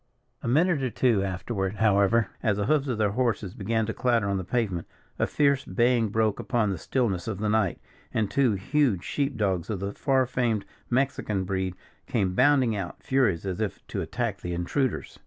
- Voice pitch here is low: Yes, low, 110 Hz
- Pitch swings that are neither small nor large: Yes, average, 4.4 semitones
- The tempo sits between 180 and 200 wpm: Yes, average, 195 wpm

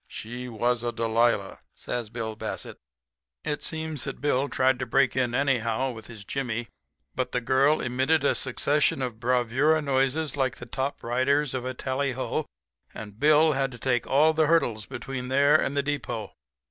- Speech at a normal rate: Yes, average, 175 wpm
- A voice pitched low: Yes, low, 130 Hz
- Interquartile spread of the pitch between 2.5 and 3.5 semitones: Yes, average, 2.9 semitones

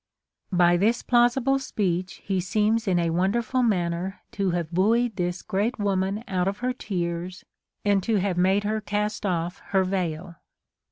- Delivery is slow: No, average, 160 wpm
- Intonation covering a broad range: No, average, 3.3 semitones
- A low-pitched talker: No, high, 195 Hz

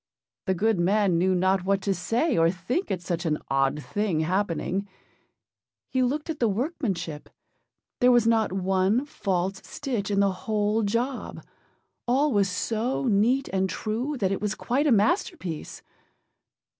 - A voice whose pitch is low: No, high, 205 Hz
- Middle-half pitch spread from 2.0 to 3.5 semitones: No, average, 4.6 semitones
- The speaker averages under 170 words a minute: Yes, average, 155 wpm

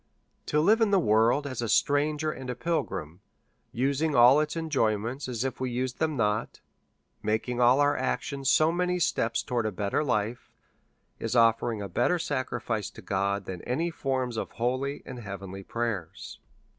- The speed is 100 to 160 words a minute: No, average, 180 wpm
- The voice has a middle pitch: No, low, 125 Hz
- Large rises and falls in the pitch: No, average, 4.8 semitones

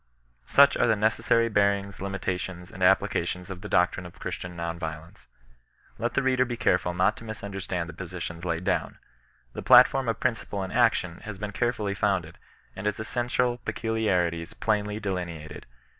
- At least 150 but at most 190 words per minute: Yes, average, 170 wpm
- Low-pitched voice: Yes, low, 100 Hz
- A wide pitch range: No, average, 3.9 semitones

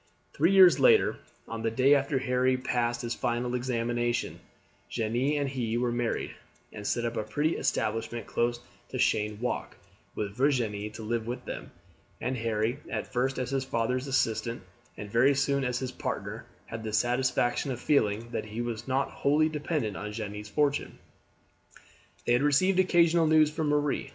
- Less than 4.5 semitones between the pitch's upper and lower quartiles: Yes, average, 3.4 semitones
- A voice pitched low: Yes, low, 125 Hz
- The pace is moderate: Yes, average, 170 wpm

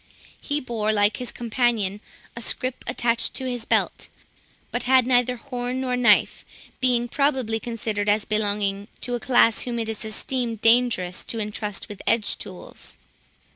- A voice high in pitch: Yes, high, 235 Hz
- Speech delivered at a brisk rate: No, average, 155 wpm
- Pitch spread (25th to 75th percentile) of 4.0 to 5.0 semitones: No, average, 2.7 semitones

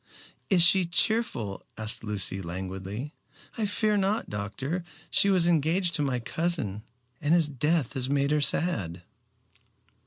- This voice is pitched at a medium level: Yes, medium, 145 Hz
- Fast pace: No, slow, 135 wpm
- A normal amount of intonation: No, wide, 8.7 semitones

